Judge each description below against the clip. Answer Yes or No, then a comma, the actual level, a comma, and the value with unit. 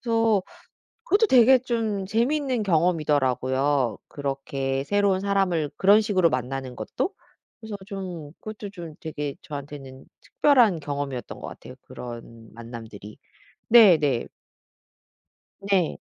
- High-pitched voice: No, medium, 165 Hz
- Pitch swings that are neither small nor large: No, wide, 7.4 semitones